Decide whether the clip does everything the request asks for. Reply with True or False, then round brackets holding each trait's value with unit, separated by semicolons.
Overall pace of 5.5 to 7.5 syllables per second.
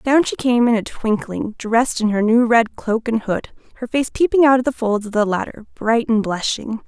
False (5.0 syllables/s)